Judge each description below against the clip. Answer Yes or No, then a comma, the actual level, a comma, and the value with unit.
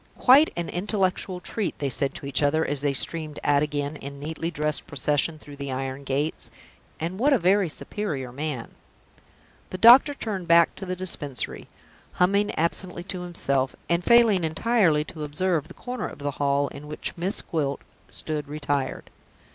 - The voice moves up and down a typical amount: Yes, average, 4.5 semitones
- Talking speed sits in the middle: Yes, average, 170 wpm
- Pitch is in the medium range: Yes, medium, 155 Hz